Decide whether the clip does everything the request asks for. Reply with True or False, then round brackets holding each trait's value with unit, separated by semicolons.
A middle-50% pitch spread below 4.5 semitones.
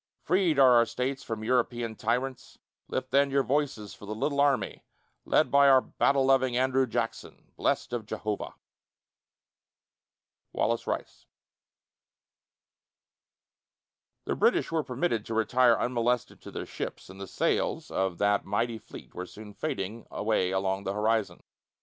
True (3.8 semitones)